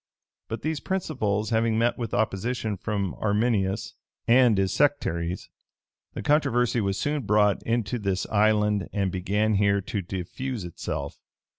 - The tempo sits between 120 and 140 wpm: Yes, slow, 135 wpm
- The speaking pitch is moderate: No, low, 105 Hz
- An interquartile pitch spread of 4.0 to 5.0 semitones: No, average, 3.5 semitones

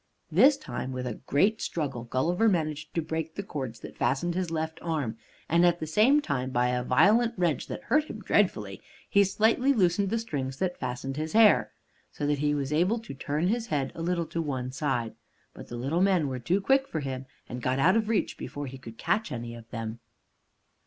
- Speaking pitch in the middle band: Yes, medium, 155 Hz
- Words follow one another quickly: Yes, fast, 215 wpm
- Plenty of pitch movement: Yes, wide, 7.0 semitones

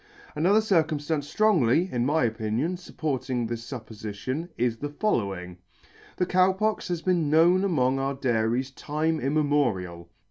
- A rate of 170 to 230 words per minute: No, slow, 135 wpm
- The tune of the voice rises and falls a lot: Yes, wide, 6.1 semitones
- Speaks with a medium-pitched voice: Yes, medium, 145 Hz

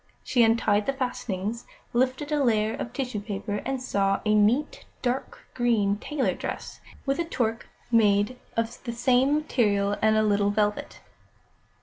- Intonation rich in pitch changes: No, average, 3.7 semitones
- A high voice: Yes, high, 230 Hz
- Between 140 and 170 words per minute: Yes, average, 150 wpm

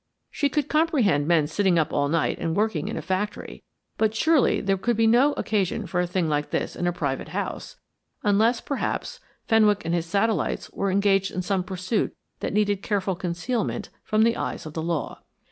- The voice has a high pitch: Yes, high, 195 Hz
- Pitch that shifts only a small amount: No, average, 4.3 semitones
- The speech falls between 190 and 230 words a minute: Yes, average, 195 wpm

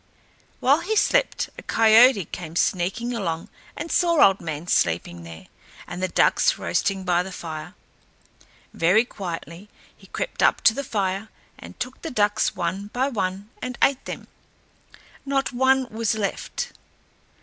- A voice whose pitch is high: Yes, high, 205 Hz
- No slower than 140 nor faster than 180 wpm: Yes, average, 150 wpm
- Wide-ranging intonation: Yes, wide, 6.2 semitones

